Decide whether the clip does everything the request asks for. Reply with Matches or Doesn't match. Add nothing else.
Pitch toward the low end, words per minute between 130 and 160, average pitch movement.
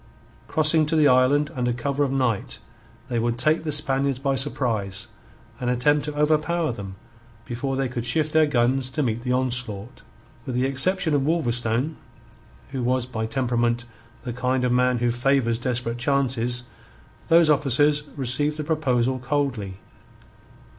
Matches